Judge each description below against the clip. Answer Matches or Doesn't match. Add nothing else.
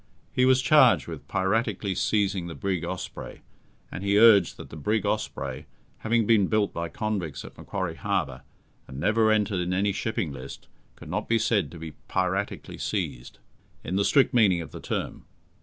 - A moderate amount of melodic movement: Matches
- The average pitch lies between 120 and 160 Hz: Doesn't match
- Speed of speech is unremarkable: Matches